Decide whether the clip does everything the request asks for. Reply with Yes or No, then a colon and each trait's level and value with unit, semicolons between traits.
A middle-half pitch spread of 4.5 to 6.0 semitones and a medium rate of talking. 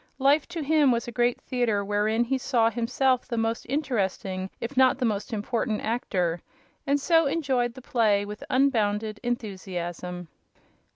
No: average, 4.1 semitones; average, 155 wpm